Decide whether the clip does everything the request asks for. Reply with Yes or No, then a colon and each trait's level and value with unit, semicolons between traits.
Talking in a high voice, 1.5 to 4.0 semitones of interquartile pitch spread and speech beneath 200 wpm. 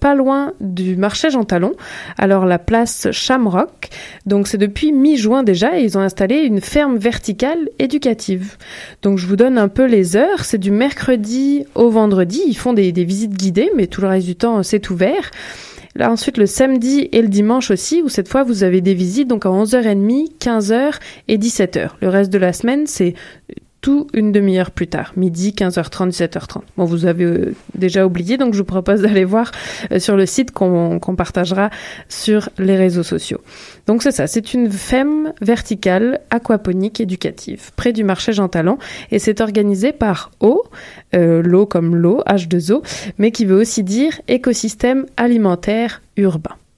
No: high, 210 Hz; average, 4.5 semitones; average, 180 wpm